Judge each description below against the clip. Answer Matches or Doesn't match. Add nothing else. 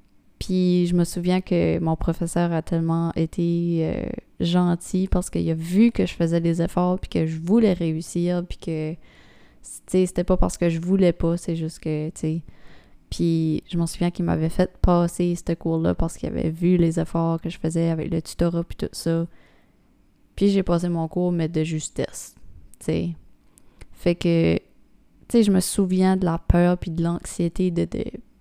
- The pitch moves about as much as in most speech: Doesn't match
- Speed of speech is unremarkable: Matches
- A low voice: Doesn't match